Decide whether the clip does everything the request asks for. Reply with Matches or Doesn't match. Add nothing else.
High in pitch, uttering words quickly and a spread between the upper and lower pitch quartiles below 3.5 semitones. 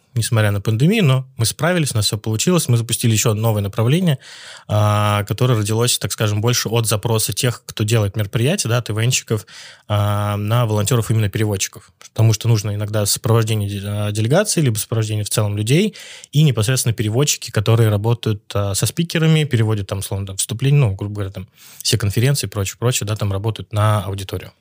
Doesn't match